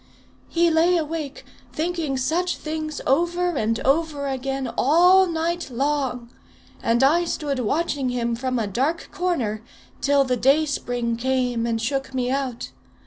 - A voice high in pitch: Yes, very high, 275 Hz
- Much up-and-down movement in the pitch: No, average, 4.6 semitones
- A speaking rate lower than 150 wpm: Yes, average, 140 wpm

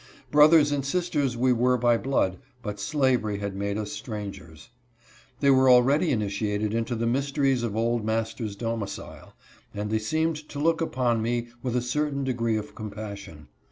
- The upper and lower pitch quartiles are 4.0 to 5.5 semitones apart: Yes, average, 4.4 semitones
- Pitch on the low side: Yes, low, 120 Hz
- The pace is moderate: Yes, average, 170 wpm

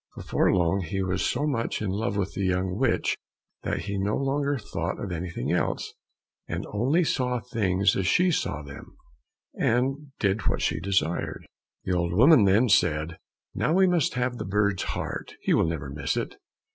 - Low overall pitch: Yes, low, 100 Hz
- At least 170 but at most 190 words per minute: Yes, average, 180 wpm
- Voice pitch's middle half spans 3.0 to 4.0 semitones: No, wide, 5.6 semitones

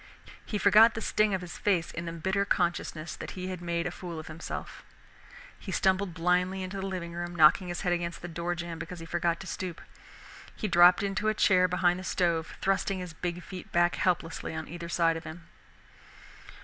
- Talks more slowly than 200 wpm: No, fast, 205 wpm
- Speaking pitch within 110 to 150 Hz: No, medium, 175 Hz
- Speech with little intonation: Yes, narrow, 1.7 semitones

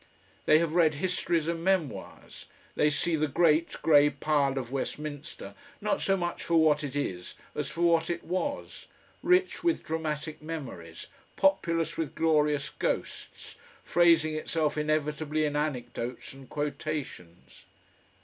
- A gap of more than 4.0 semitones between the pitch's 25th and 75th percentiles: No, narrow, 2.4 semitones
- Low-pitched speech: No, medium, 155 Hz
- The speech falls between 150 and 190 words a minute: No, slow, 135 wpm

